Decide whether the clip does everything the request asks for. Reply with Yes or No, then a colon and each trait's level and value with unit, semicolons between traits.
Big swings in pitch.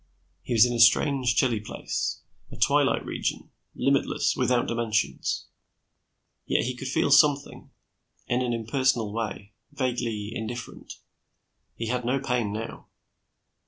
No: narrow, 2.4 semitones